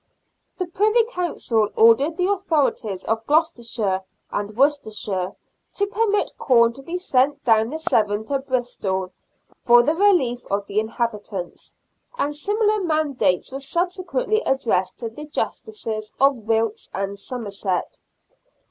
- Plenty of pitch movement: Yes, wide, 7.6 semitones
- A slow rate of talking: Yes, slow, 130 wpm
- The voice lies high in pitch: Yes, very high, 255 Hz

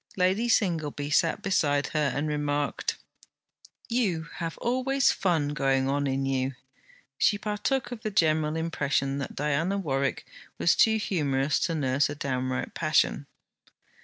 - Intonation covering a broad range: Yes, wide, 5.7 semitones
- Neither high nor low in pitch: Yes, medium, 150 Hz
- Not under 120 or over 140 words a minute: Yes, slow, 135 wpm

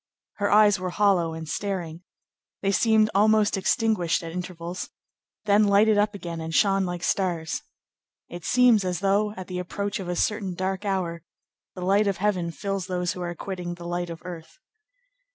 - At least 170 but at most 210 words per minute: Yes, average, 175 wpm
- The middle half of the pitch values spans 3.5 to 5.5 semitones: No, average, 2.8 semitones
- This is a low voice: No, medium, 185 Hz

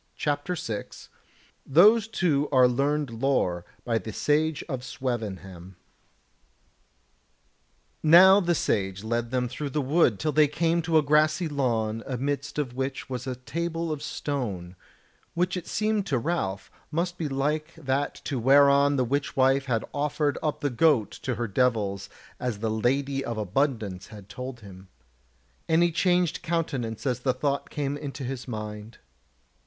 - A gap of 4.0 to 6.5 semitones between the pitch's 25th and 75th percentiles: Yes, average, 4.7 semitones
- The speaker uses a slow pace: No, average, 155 wpm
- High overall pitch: No, low, 135 Hz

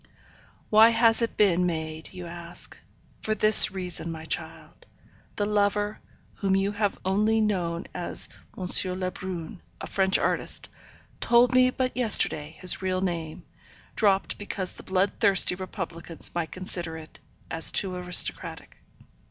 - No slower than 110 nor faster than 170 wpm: Yes, slow, 135 wpm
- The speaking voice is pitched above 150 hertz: Yes, medium, 185 Hz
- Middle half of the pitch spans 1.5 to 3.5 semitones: Yes, average, 3.2 semitones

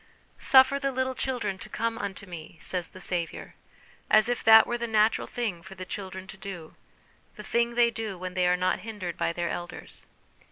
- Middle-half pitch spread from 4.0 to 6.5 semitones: Yes, average, 4.4 semitones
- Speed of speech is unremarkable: No, fast, 215 wpm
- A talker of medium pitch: No, high, 205 Hz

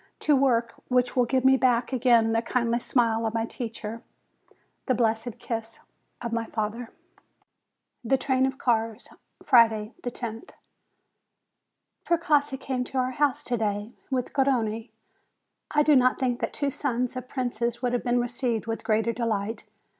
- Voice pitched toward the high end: Yes, high, 240 Hz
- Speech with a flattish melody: Yes, narrow, 2.2 semitones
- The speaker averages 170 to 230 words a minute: No, average, 155 wpm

